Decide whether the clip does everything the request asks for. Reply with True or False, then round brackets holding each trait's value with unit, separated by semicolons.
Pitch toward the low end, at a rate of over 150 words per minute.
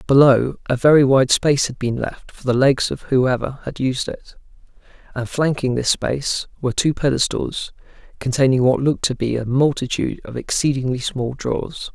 True (130 Hz; 170 wpm)